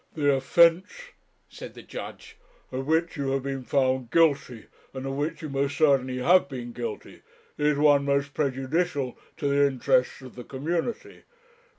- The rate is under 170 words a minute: Yes, average, 160 wpm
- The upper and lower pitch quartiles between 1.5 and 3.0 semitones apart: Yes, narrow, 2.6 semitones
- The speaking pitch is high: No, medium, 140 Hz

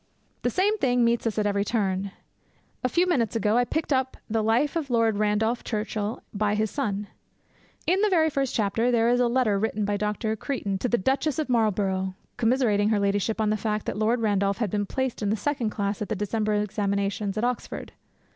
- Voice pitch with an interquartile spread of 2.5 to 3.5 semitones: Yes, average, 3.1 semitones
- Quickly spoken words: Yes, fast, 210 wpm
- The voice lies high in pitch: Yes, high, 220 Hz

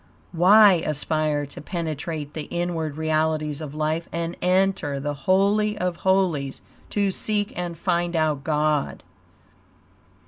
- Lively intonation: No, average, 3.1 semitones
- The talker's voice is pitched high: No, medium, 160 Hz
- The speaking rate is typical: No, slow, 125 wpm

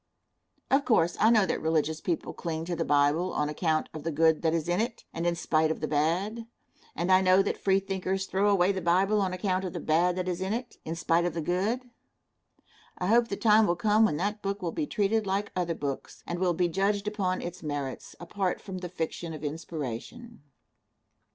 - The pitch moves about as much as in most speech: Yes, average, 3.6 semitones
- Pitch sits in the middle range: Yes, medium, 180 Hz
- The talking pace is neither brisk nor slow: No, fast, 215 wpm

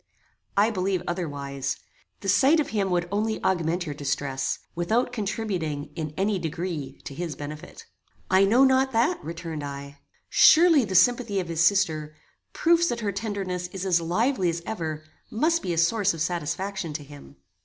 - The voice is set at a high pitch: No, medium, 180 Hz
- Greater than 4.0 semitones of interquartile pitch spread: Yes, wide, 5.4 semitones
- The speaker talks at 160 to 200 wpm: Yes, average, 165 wpm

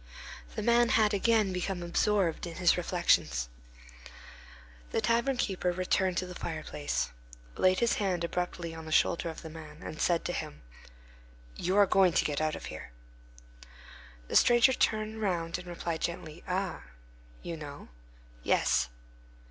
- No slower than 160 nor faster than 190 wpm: No, average, 150 wpm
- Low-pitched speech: No, medium, 180 Hz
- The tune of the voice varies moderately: Yes, average, 3.4 semitones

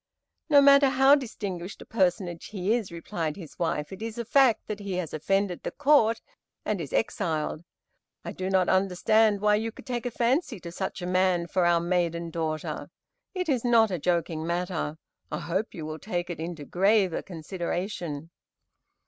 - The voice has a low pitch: No, medium, 185 Hz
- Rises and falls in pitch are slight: No, average, 4.6 semitones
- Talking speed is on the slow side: No, average, 180 wpm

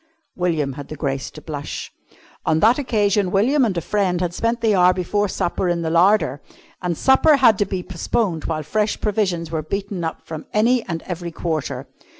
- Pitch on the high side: No, medium, 180 Hz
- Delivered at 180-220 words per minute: Yes, average, 190 wpm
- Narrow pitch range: No, average, 4.6 semitones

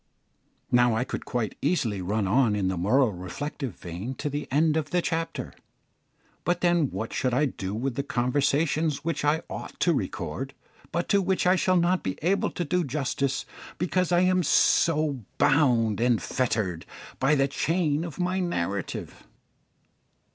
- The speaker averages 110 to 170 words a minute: Yes, average, 165 wpm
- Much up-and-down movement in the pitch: Yes, wide, 6.4 semitones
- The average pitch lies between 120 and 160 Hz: Yes, medium, 140 Hz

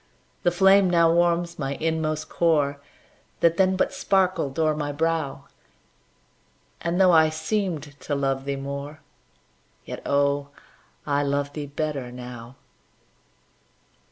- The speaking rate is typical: No, slow, 125 wpm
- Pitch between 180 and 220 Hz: No, medium, 155 Hz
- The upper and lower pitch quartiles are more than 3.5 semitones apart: No, average, 3.2 semitones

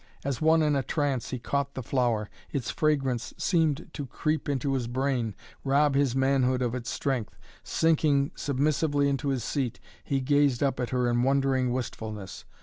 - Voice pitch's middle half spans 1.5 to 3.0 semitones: Yes, narrow, 2.4 semitones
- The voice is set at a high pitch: No, low, 135 Hz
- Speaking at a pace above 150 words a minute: Yes, average, 170 wpm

